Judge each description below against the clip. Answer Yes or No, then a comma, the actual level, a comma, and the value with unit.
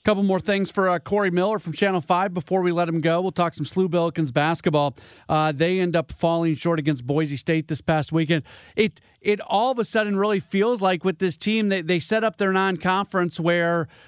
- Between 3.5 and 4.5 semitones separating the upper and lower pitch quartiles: No, average, 3.1 semitones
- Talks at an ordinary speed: No, fast, 225 wpm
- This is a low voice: No, medium, 180 Hz